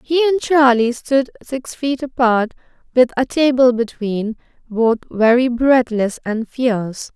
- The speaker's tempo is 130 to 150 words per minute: Yes, slow, 135 wpm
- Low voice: No, high, 245 Hz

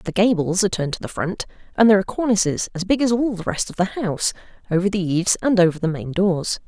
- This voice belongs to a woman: Yes, female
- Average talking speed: No, fast, 250 wpm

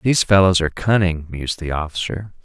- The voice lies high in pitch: No, very low, 90 Hz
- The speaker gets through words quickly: No, average, 170 wpm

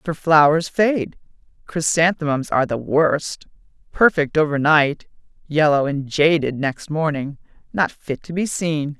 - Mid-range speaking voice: Yes, medium, 155 Hz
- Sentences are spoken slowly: Yes, slow, 125 wpm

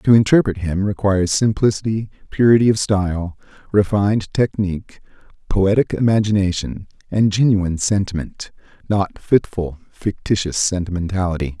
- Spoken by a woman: No, male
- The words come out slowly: Yes, slow, 95 wpm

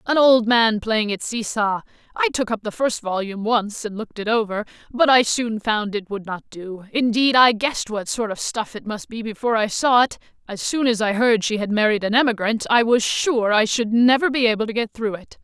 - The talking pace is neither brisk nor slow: No, fast, 240 wpm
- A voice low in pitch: No, high, 225 Hz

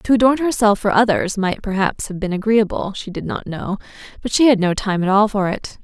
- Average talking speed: No, fast, 215 wpm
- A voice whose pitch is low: No, high, 210 Hz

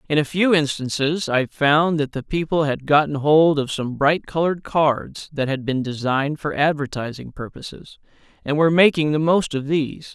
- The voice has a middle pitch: Yes, medium, 150 Hz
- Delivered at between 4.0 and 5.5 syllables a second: Yes, 5.0 syllables/s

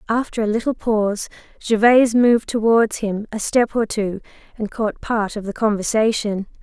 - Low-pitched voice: No, high, 220 Hz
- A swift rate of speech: No, average, 165 wpm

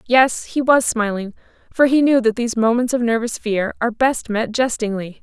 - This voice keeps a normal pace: Yes, average, 195 wpm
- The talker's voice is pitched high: Yes, high, 235 Hz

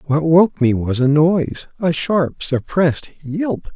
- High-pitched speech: No, medium, 155 Hz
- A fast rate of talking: No, average, 145 wpm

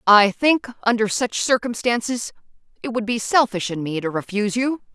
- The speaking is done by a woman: Yes, female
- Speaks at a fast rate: No, average, 170 wpm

